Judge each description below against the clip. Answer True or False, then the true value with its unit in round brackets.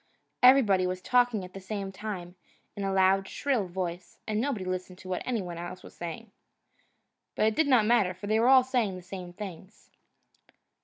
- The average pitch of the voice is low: False (195 Hz)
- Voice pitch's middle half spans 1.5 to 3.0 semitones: False (3.7 semitones)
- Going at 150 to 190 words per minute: True (185 wpm)